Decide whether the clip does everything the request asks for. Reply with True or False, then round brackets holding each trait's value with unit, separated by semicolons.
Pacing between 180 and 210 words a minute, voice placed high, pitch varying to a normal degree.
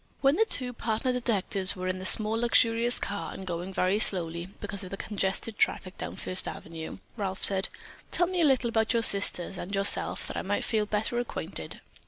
True (200 wpm; 205 Hz; 3.8 semitones)